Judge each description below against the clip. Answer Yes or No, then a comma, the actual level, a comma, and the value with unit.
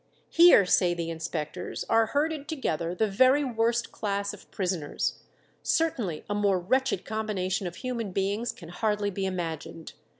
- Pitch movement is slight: No, average, 4.8 semitones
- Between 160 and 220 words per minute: No, average, 145 wpm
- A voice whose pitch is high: Yes, high, 200 Hz